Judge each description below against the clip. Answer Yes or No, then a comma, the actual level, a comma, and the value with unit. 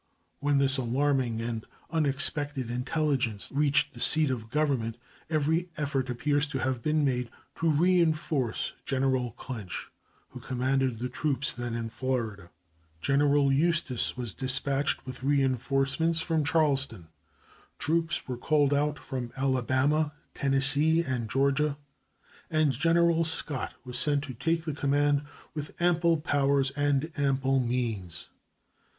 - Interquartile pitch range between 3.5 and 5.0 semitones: No, average, 2.9 semitones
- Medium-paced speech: No, slow, 125 wpm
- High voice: No, medium, 140 Hz